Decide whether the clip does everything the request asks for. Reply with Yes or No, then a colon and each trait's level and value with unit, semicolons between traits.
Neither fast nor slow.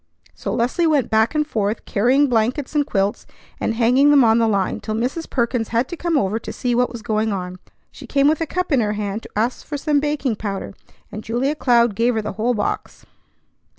No: fast, 220 wpm